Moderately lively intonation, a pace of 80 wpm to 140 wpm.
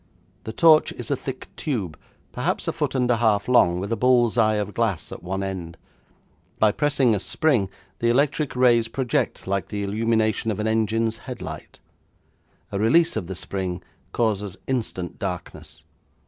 No: average, 3.9 semitones; average, 165 wpm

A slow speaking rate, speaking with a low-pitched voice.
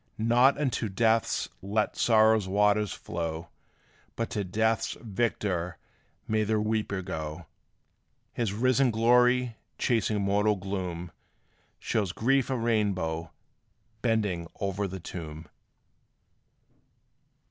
Yes: slow, 100 wpm; low, 105 Hz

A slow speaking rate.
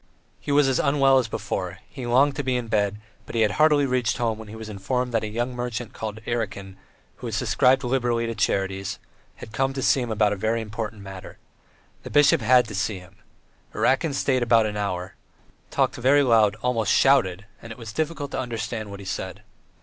No: fast, 205 wpm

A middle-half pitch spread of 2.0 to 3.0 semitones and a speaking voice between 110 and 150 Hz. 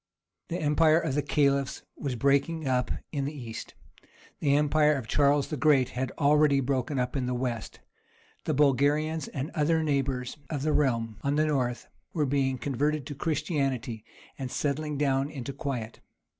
Yes: narrow, 2.4 semitones; medium, 140 Hz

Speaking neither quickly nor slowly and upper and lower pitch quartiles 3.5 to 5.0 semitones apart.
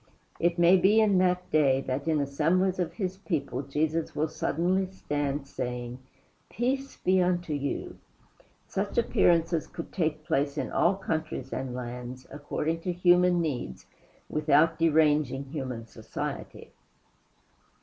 No: slow, 130 wpm; average, 4.3 semitones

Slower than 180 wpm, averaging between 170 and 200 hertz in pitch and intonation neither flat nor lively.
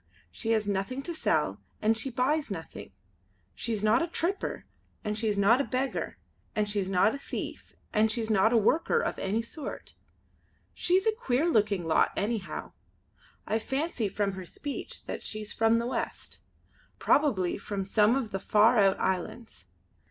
No: average, 165 wpm; high, 220 Hz; average, 4.4 semitones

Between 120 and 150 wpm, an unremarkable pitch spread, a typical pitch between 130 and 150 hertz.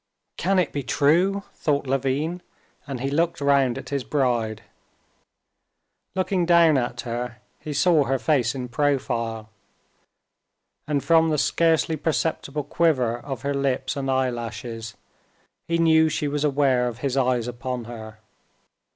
Yes: average, 140 wpm; average, 4.2 semitones; medium, 140 Hz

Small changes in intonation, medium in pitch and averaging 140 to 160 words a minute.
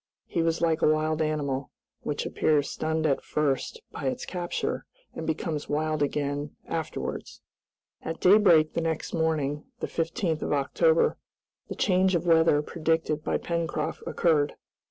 Yes: narrow, 2.0 semitones; medium, 160 Hz; average, 145 wpm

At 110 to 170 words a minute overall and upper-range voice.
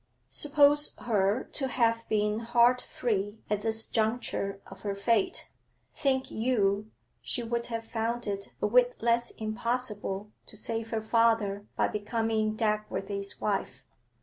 Yes: slow, 135 wpm; high, 225 Hz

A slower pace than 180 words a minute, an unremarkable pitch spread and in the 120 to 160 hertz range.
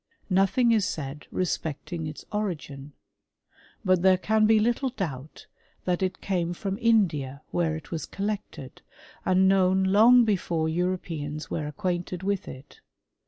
No: slow, 135 wpm; average, 4.2 semitones; medium, 185 Hz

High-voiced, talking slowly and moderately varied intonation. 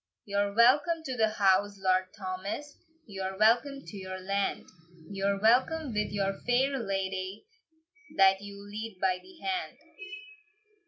Yes: high, 200 Hz; slow, 130 wpm; average, 4.2 semitones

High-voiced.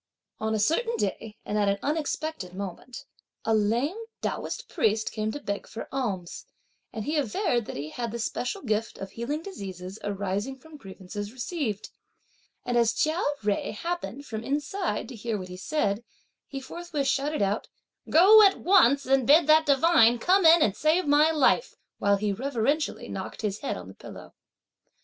Yes: high, 240 Hz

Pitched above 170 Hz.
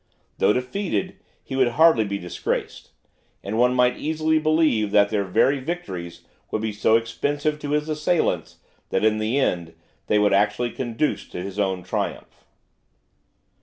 No: low, 115 Hz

